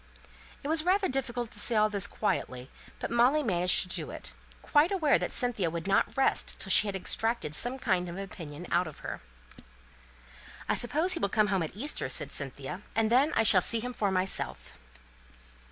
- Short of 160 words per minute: No, average, 200 wpm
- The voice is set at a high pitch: Yes, high, 215 Hz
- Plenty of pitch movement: Yes, wide, 6.0 semitones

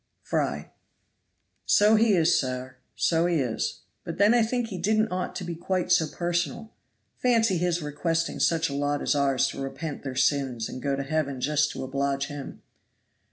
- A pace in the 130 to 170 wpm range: No, average, 180 wpm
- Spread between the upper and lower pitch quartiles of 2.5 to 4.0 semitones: No, average, 4.6 semitones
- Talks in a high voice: No, medium, 160 Hz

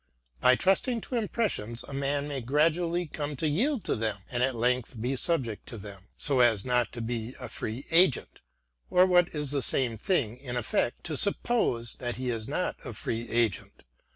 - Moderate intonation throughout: No, wide, 5.8 semitones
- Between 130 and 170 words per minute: No, average, 185 wpm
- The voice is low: Yes, low, 130 Hz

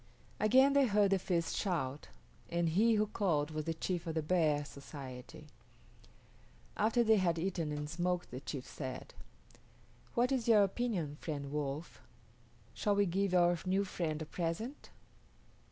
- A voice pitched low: No, medium, 175 Hz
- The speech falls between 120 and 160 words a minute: Yes, average, 155 wpm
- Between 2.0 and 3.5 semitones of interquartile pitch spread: No, average, 5.1 semitones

